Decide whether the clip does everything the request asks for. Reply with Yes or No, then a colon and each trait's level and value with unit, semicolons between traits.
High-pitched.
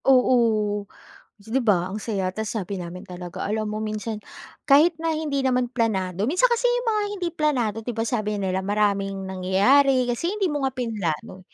Yes: high, 220 Hz